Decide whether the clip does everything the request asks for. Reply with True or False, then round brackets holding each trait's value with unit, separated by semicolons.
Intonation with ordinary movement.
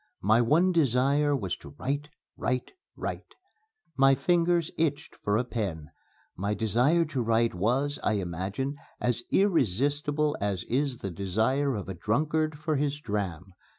False (6.2 semitones)